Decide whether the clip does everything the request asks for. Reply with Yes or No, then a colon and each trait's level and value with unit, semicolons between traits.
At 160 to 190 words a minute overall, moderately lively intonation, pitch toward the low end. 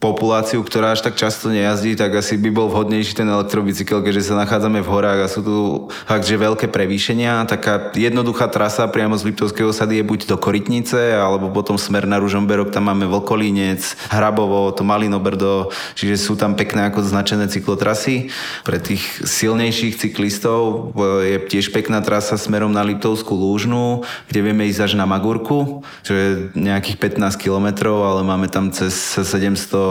No: fast, 165 wpm; narrow, 1.6 semitones; low, 105 Hz